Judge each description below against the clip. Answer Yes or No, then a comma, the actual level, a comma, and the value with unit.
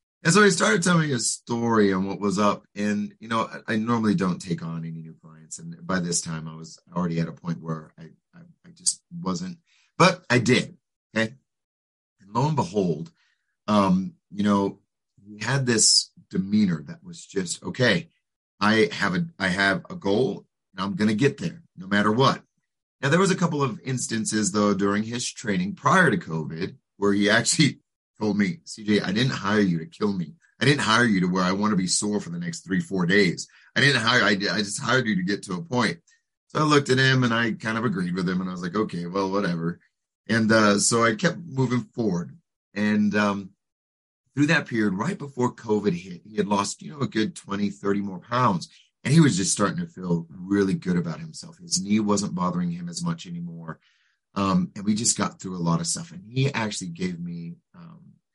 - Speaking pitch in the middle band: No, low, 115 Hz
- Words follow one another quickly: Yes, fast, 215 wpm